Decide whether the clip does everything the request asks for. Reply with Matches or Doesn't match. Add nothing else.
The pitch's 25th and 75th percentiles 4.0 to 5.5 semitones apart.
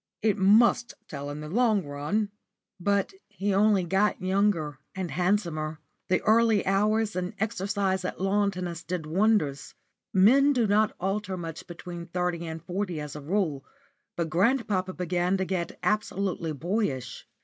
Doesn't match